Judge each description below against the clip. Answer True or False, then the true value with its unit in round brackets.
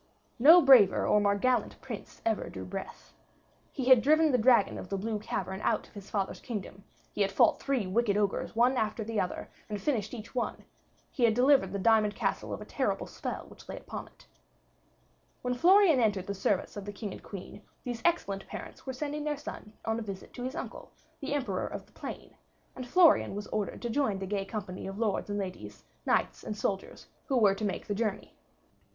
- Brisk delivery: True (210 wpm)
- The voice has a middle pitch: False (215 Hz)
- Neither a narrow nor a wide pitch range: True (4.3 semitones)